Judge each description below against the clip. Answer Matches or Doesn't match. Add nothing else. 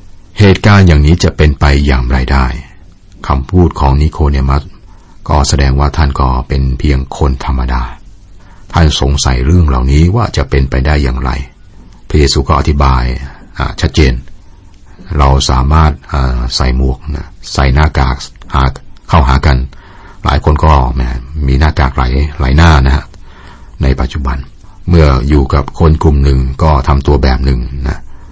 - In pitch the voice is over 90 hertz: Doesn't match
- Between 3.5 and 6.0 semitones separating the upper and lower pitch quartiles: Matches